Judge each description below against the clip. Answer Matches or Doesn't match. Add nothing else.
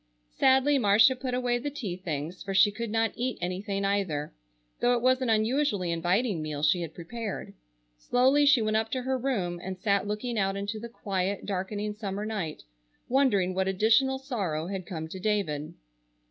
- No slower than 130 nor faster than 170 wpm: Doesn't match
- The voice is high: Matches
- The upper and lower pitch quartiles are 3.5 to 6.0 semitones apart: Matches